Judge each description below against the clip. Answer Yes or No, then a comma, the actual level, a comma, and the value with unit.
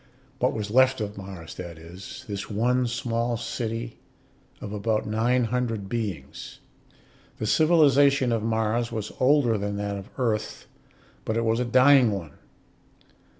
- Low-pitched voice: Yes, low, 115 Hz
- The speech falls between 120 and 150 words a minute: Yes, average, 145 wpm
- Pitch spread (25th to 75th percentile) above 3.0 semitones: Yes, average, 3.4 semitones